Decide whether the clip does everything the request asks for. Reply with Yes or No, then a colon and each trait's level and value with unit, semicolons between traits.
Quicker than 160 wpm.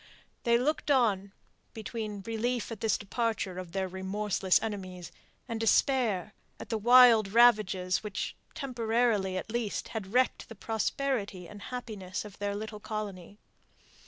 No: slow, 135 wpm